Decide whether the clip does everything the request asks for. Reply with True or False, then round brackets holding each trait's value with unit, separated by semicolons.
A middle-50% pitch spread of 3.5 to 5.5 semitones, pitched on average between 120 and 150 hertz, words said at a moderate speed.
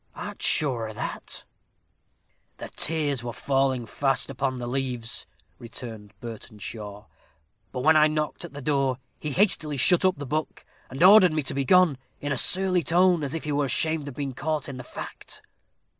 True (3.8 semitones; 140 Hz; 180 wpm)